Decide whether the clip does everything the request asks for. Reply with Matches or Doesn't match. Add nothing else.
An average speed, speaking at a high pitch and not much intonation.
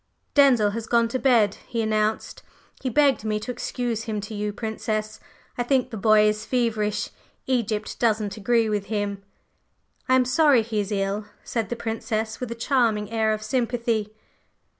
Matches